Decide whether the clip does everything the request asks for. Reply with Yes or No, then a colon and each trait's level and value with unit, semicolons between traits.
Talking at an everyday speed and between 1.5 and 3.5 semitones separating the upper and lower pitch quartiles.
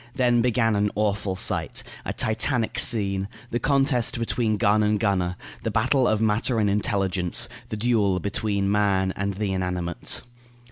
Yes: average, 150 wpm; average, 2.8 semitones